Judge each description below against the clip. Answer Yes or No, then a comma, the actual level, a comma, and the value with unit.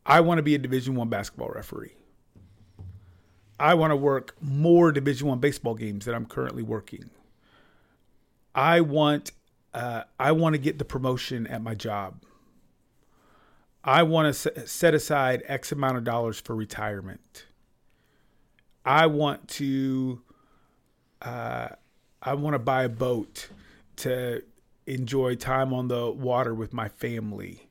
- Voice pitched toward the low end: Yes, low, 130 Hz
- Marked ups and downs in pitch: No, average, 4.3 semitones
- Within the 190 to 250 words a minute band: No, average, 140 wpm